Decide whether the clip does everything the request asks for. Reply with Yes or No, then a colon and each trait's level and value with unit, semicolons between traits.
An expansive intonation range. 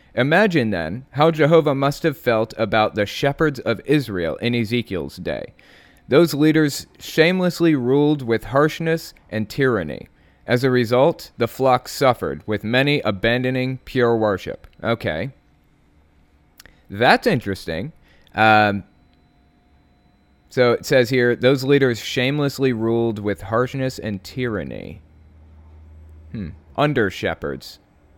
Yes: wide, 6.0 semitones